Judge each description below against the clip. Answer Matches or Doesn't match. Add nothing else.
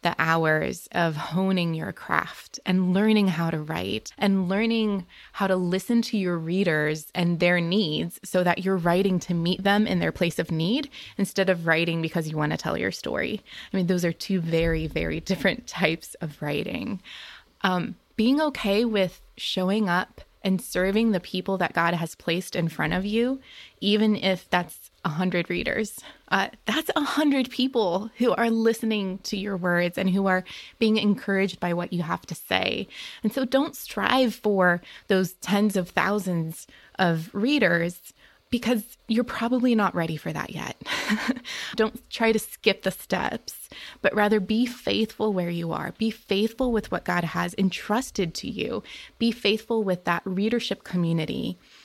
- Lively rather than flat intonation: Doesn't match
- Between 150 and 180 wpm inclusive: Matches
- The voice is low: Doesn't match